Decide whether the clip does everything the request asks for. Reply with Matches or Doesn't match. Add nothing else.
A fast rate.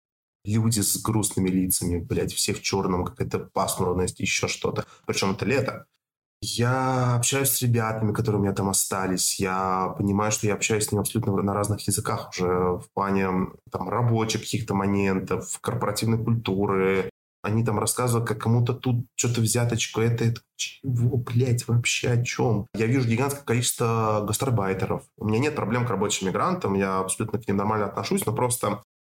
Matches